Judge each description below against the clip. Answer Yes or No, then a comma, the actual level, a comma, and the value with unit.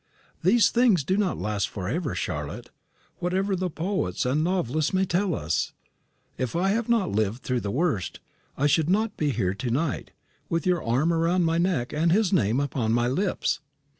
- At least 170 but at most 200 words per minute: Yes, average, 185 wpm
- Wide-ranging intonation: Yes, wide, 7.3 semitones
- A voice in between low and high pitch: Yes, medium, 165 Hz